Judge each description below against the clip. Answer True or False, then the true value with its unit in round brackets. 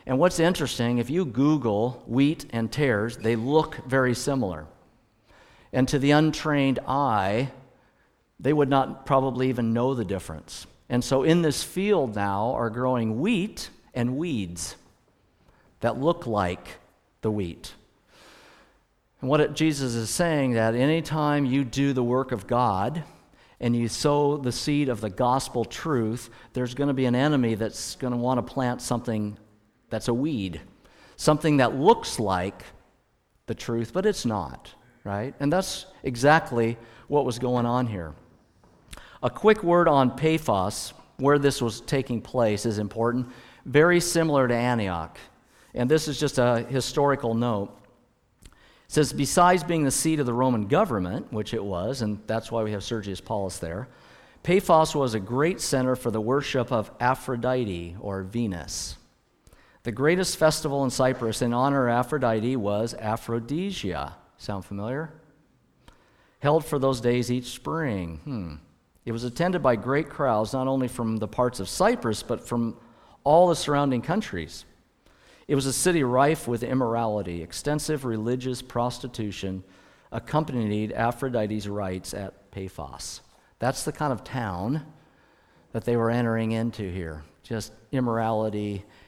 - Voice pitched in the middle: False (125 Hz)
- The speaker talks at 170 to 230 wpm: False (150 wpm)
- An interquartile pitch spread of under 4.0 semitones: False (4.5 semitones)